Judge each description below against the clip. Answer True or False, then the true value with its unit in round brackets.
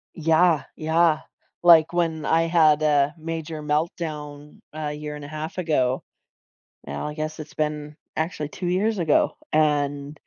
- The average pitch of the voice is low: False (155 Hz)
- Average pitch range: False (1.7 semitones)